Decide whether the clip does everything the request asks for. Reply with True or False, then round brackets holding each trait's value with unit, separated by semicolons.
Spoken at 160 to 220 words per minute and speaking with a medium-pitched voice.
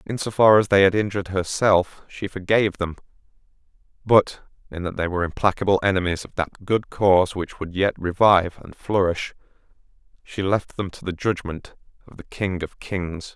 False (175 wpm; 95 Hz)